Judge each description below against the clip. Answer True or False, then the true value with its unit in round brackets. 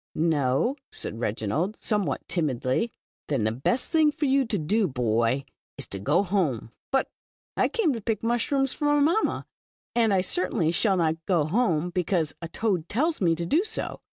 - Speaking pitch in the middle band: True (180 Hz)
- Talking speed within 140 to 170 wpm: False (190 wpm)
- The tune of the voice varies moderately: False (8.2 semitones)